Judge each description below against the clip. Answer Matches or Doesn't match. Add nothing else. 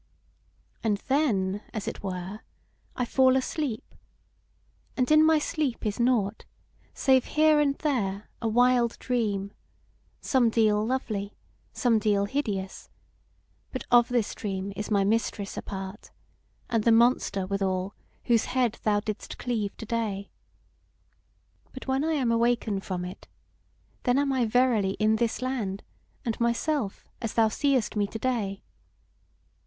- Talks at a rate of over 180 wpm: Doesn't match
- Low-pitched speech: Doesn't match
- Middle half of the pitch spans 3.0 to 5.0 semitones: Matches